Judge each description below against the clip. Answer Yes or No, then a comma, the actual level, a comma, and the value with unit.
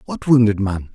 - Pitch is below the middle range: Yes, low, 110 Hz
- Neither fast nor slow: Yes, average, 190 wpm